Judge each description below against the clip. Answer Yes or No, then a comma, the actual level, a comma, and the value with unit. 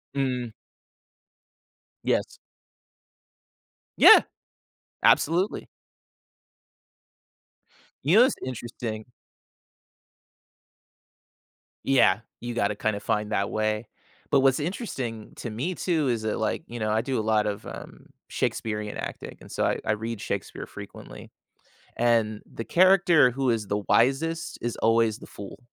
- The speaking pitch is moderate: No, low, 115 Hz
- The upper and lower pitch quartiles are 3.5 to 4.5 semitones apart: Yes, average, 4.1 semitones